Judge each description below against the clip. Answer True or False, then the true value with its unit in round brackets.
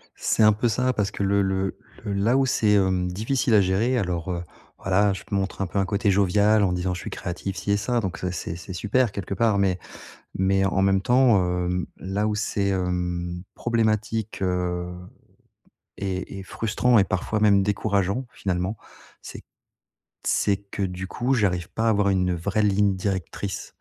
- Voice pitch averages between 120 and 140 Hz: False (100 Hz)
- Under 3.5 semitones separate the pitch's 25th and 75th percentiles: True (2.5 semitones)